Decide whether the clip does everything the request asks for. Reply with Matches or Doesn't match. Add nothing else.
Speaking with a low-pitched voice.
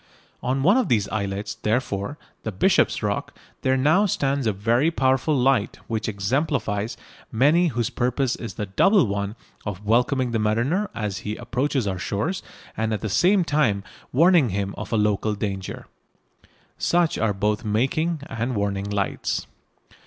Matches